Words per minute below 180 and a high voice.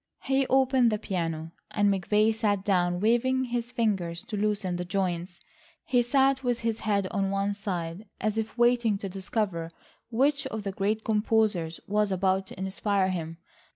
Yes: average, 165 wpm; high, 205 Hz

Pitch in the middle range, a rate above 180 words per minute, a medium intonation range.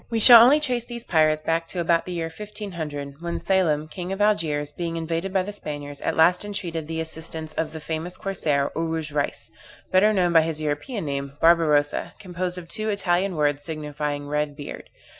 Yes: medium, 165 Hz; average, 195 wpm; average, 3.8 semitones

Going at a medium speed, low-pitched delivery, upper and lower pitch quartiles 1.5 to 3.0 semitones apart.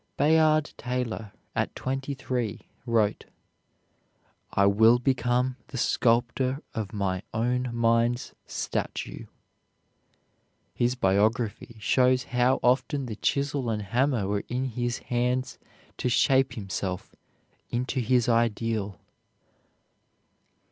No: slow, 100 wpm; low, 120 Hz; narrow, 2.6 semitones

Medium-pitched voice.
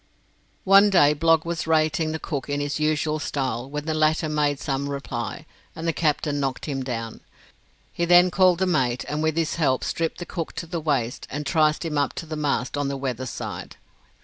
Yes: medium, 150 Hz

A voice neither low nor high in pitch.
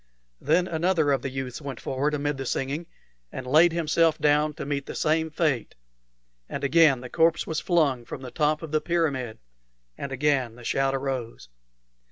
Yes: medium, 145 Hz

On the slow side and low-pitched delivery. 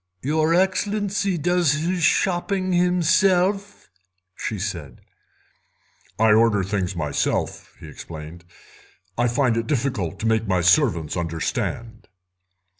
Yes: slow, 115 wpm; low, 125 Hz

